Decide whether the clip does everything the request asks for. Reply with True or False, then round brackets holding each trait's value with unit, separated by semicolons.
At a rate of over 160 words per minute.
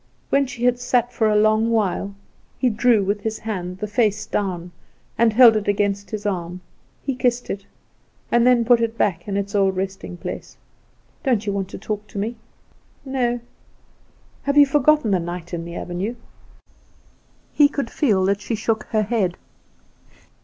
True (175 wpm)